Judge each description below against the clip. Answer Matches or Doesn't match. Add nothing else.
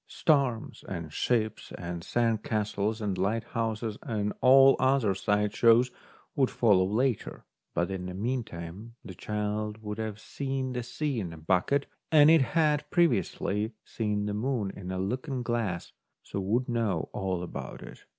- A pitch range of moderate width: Matches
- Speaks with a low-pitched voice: Matches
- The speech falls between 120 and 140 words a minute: Doesn't match